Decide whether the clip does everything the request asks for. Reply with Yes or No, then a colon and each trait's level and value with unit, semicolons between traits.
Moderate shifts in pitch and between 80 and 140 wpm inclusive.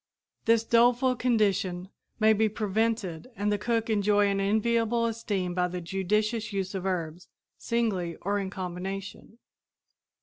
Yes: average, 3.2 semitones; slow, 135 wpm